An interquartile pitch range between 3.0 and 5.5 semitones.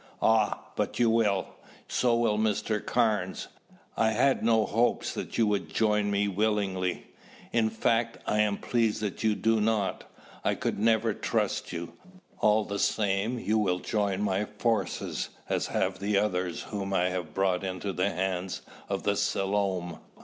No: narrow, 2.5 semitones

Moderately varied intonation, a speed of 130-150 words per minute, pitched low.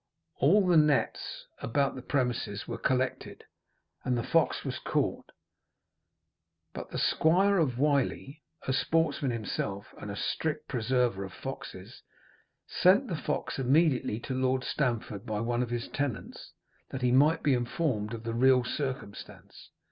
Yes: average, 3.5 semitones; average, 145 wpm; low, 130 Hz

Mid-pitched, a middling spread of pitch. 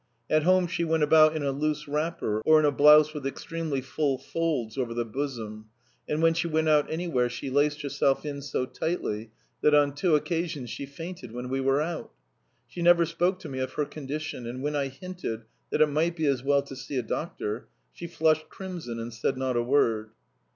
Yes: medium, 145 Hz; average, 3.6 semitones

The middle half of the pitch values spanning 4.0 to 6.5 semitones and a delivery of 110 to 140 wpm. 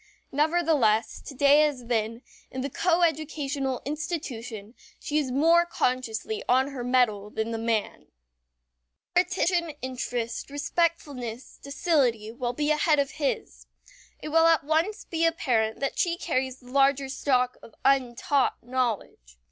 Yes: average, 4.3 semitones; slow, 135 wpm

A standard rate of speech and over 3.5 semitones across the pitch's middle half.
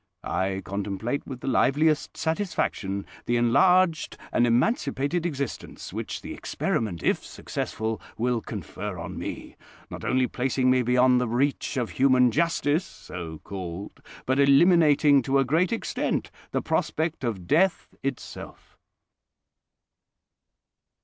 No: slow, 125 wpm; average, 5.0 semitones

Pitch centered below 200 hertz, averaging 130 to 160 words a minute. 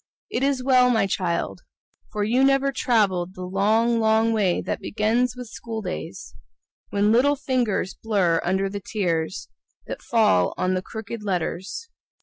No: high, 215 Hz; average, 150 wpm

